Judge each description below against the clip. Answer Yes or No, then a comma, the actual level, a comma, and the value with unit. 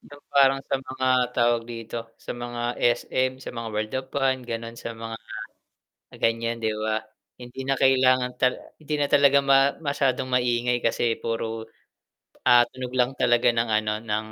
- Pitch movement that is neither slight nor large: No, narrow, 2.2 semitones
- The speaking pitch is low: Yes, low, 120 Hz